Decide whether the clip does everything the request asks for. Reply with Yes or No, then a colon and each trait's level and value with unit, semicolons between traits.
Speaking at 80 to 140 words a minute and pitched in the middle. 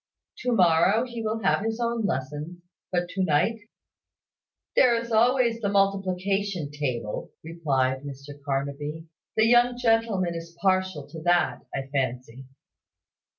Yes: slow, 135 wpm; medium, 180 Hz